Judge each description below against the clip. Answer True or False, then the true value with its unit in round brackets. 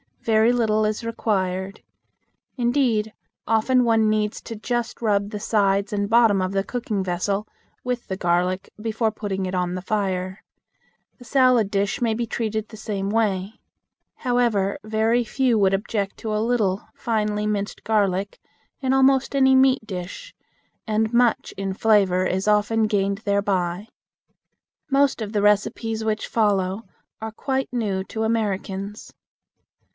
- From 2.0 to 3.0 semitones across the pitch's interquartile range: True (2.6 semitones)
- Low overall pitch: False (215 Hz)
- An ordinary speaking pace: True (145 wpm)